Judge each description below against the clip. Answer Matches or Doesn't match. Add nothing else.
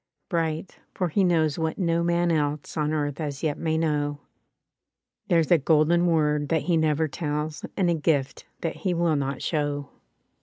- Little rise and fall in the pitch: Matches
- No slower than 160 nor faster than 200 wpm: Matches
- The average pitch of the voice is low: Doesn't match